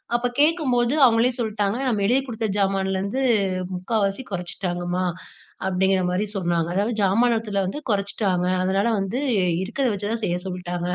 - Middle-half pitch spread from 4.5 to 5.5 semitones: No, average, 3.8 semitones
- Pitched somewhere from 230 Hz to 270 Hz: No, high, 200 Hz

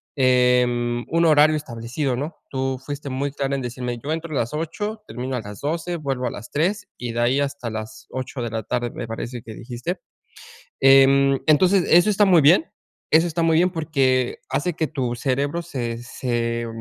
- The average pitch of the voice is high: No, low, 135 Hz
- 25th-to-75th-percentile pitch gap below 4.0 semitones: No, average, 4.5 semitones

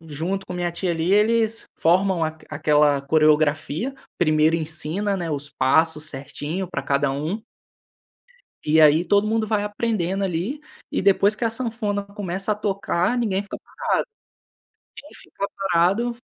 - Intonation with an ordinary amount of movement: Yes, average, 4.9 semitones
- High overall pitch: No, medium, 180 Hz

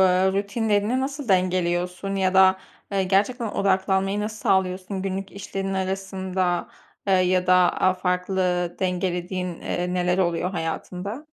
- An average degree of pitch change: No, narrow, 1.4 semitones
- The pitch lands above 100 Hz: Yes, high, 190 Hz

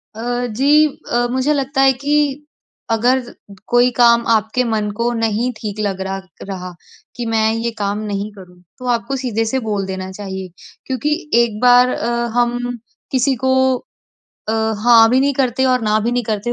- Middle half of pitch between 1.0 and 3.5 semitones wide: Yes, average, 3.2 semitones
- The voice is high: Yes, high, 235 Hz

